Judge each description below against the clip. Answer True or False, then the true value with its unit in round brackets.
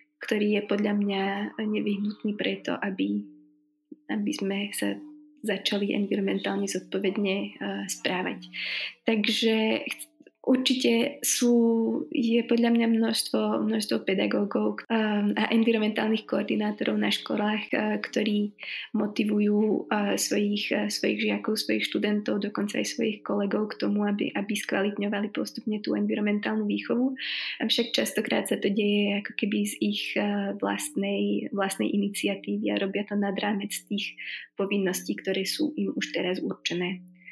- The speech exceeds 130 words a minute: False (120 wpm)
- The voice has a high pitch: True (205 Hz)